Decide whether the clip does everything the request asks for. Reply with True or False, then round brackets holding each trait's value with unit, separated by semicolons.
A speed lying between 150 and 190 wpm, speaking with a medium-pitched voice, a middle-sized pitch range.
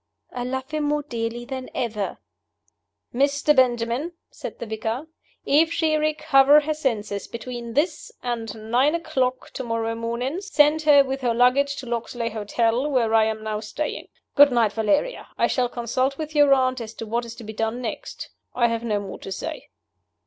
False (180 wpm; 245 Hz; 3.9 semitones)